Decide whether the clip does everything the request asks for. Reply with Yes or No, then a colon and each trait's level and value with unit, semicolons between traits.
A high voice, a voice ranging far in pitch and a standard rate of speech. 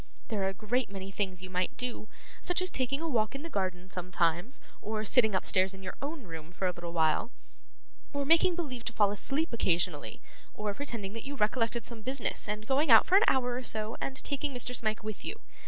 No: high, 220 Hz; wide, 5.7 semitones; fast, 220 wpm